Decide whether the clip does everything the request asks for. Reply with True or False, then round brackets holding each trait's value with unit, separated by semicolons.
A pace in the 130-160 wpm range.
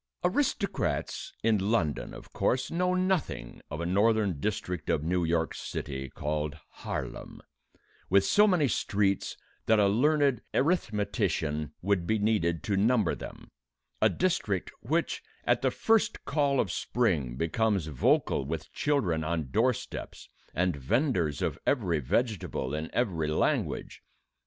True (135 wpm)